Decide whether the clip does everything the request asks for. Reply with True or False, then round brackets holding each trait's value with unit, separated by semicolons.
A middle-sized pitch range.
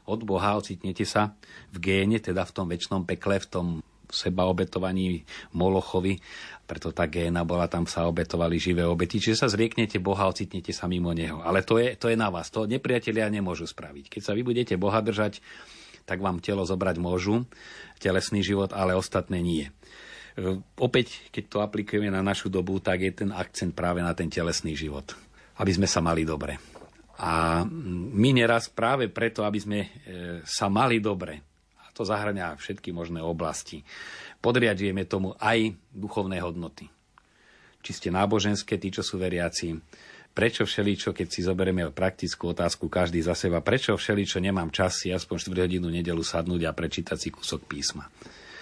True (3.3 semitones)